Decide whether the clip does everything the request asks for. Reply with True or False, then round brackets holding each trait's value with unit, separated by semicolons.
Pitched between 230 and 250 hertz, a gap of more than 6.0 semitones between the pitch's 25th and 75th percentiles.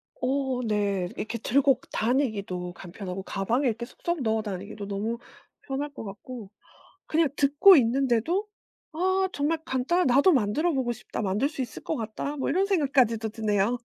False (245 Hz; 5.2 semitones)